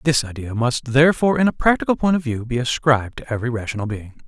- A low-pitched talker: Yes, low, 130 Hz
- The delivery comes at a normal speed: No, fast, 225 wpm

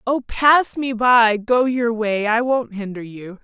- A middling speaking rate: Yes, average, 190 wpm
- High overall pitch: Yes, high, 230 Hz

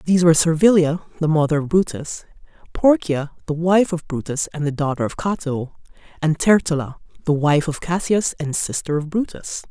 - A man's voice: No, female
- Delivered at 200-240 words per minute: No, average, 165 wpm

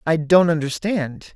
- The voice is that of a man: Yes, male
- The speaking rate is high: No, slow, 135 wpm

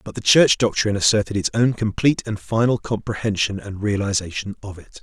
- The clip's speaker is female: No, male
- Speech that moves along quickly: No, average, 180 wpm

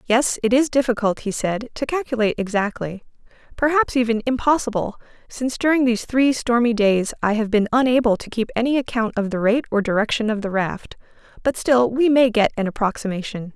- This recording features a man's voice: No, female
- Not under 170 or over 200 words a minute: Yes, average, 180 wpm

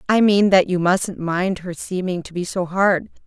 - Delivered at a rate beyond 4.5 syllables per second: No, 4.4 syllables/s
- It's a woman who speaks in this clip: Yes, female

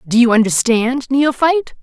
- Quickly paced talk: No, slow, 130 wpm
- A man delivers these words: No, female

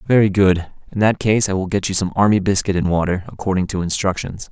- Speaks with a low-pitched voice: Yes, very low, 95 Hz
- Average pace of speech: No, fast, 225 wpm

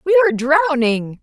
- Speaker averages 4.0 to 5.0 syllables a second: No, 5.2 syllables/s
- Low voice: No, very high, 290 Hz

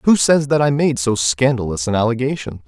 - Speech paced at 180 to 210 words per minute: Yes, average, 200 wpm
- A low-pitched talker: Yes, low, 125 Hz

